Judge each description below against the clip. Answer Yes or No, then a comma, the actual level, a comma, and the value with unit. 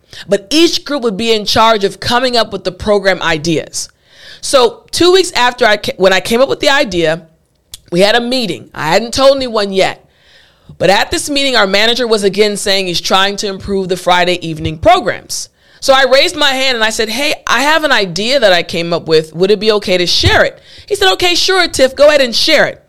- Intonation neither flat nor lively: No, wide, 6.6 semitones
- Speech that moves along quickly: Yes, fast, 230 wpm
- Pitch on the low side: No, high, 225 Hz